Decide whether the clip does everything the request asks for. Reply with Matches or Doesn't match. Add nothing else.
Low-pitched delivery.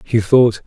Matches